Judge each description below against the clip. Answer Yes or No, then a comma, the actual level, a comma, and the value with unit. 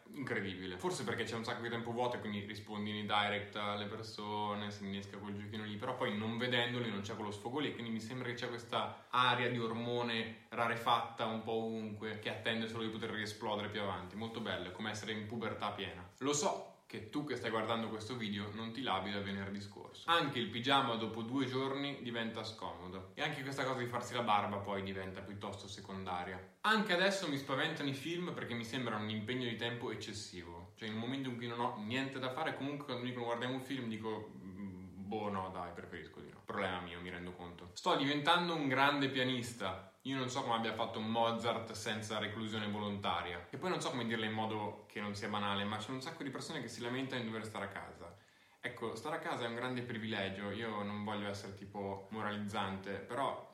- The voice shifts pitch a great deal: No, average, 3.1 semitones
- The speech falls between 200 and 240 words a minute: Yes, fast, 215 wpm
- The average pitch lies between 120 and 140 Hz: No, low, 110 Hz